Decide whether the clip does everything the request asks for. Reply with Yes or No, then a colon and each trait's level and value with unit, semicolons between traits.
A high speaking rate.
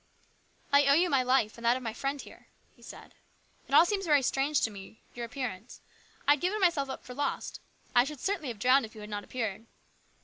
Yes: fast, 235 wpm